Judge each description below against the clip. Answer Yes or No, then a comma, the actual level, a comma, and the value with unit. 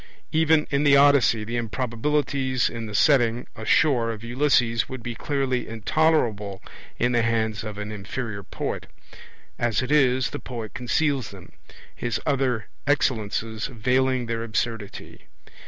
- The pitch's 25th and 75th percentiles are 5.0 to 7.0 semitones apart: No, average, 3.4 semitones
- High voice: No, low, 120 Hz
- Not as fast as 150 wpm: Yes, average, 140 wpm